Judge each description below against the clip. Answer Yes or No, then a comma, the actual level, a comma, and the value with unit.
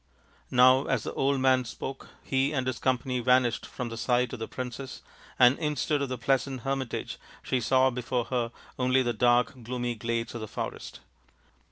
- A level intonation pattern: Yes, narrow, 1.6 semitones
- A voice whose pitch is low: Yes, low, 125 Hz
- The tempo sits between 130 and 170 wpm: No, average, 180 wpm